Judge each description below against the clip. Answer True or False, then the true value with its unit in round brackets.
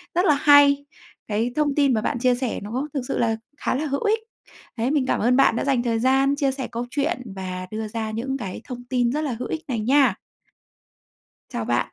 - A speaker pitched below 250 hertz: False (255 Hz)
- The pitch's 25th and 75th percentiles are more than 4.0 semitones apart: False (3.6 semitones)